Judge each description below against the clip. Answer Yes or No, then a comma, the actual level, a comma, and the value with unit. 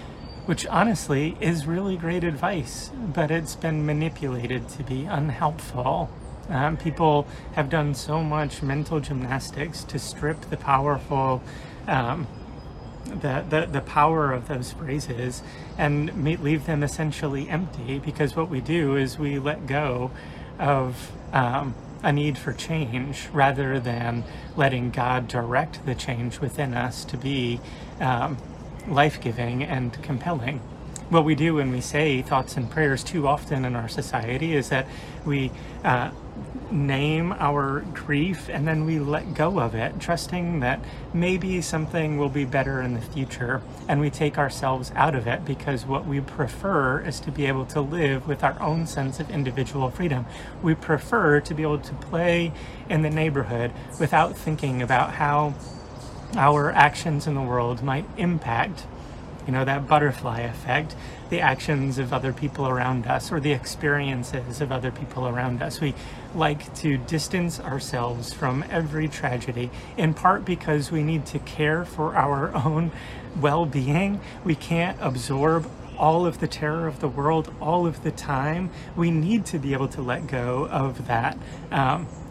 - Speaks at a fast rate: No, average, 155 wpm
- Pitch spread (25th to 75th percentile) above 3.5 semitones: No, average, 3.1 semitones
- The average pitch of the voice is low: No, medium, 145 Hz